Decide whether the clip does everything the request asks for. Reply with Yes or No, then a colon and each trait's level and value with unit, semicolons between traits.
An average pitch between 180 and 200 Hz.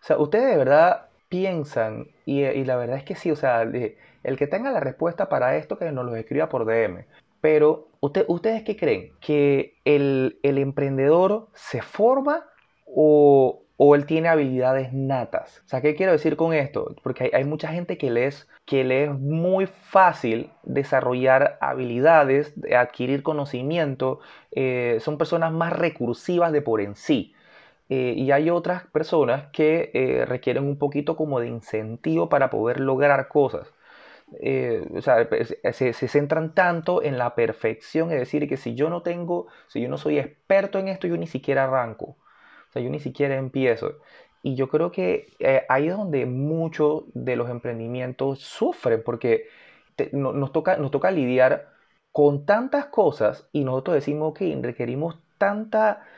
No: medium, 145 Hz